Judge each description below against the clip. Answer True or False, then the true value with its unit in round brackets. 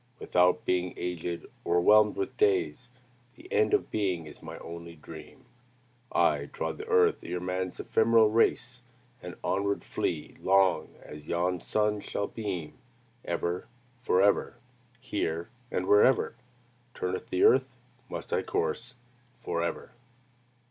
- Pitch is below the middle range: True (95 Hz)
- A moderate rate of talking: False (125 wpm)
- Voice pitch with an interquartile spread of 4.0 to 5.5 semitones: True (4.3 semitones)